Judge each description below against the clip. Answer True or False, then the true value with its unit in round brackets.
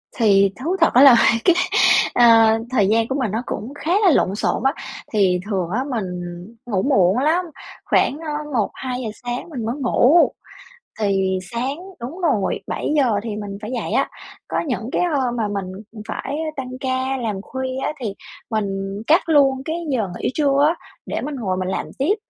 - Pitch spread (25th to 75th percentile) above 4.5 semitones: True (4.9 semitones)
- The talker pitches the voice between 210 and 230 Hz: False (245 Hz)